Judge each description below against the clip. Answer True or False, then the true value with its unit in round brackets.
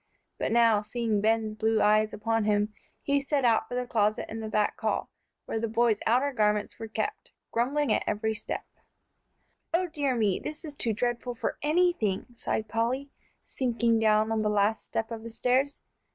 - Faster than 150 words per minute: True (180 wpm)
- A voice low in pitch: False (225 Hz)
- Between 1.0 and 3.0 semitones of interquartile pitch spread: True (2.6 semitones)